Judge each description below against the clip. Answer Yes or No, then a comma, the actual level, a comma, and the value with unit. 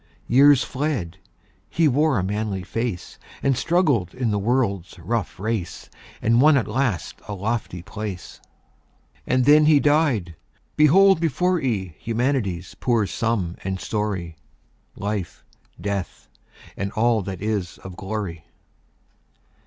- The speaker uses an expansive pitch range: Yes, wide, 5.8 semitones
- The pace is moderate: No, slow, 125 wpm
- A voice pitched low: Yes, low, 110 Hz